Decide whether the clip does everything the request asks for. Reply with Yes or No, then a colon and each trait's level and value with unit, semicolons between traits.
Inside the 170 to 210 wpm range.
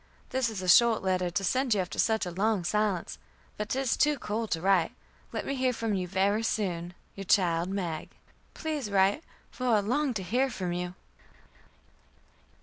Yes: average, 180 wpm